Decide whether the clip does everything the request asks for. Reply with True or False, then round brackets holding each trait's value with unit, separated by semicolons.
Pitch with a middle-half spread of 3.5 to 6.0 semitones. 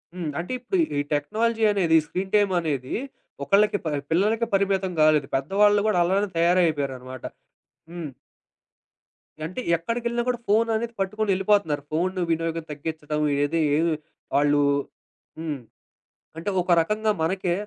True (4.9 semitones)